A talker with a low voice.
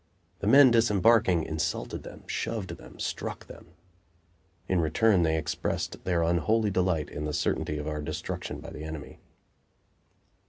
Yes: very low, 85 Hz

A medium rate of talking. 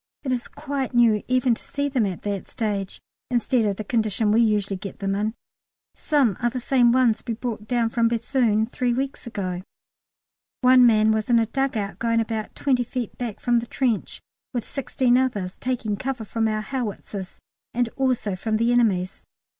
Yes: average, 185 wpm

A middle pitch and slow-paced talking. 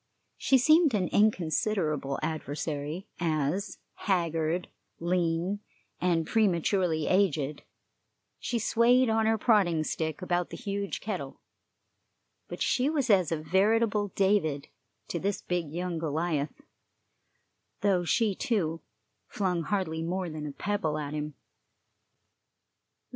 Yes: medium, 180 Hz; slow, 115 wpm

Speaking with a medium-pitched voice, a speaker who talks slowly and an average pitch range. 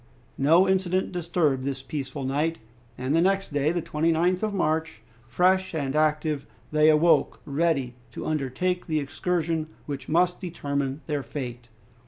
No: medium, 155 Hz; average, 145 wpm; average, 3.7 semitones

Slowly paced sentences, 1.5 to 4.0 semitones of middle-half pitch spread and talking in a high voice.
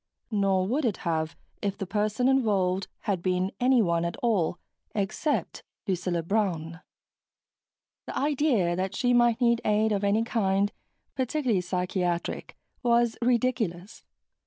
No: slow, 125 wpm; average, 4.6 semitones; high, 205 Hz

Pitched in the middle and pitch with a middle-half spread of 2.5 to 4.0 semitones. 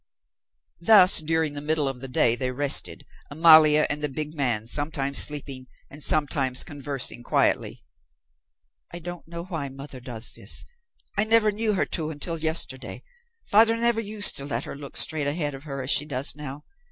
Yes: medium, 150 Hz; average, 3.4 semitones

